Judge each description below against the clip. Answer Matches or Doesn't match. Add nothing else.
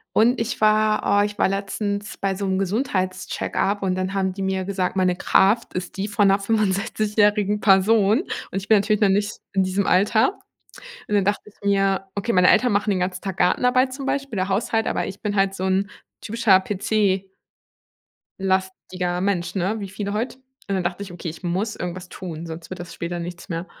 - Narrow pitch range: Matches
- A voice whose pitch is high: Matches